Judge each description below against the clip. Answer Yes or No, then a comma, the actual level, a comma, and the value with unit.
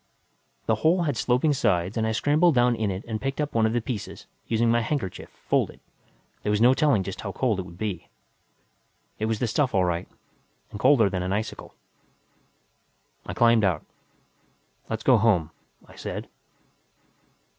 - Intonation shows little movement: No, average, 4.0 semitones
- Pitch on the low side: Yes, low, 110 Hz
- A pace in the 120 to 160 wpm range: No, average, 175 wpm